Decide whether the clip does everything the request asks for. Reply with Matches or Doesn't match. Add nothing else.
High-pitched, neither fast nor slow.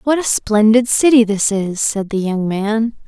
Matches